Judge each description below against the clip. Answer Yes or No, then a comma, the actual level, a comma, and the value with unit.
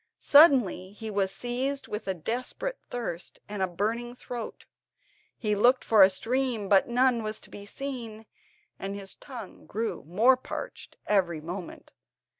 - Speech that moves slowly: No, average, 160 wpm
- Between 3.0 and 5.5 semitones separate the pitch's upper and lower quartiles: Yes, average, 4.1 semitones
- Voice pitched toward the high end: Yes, high, 220 Hz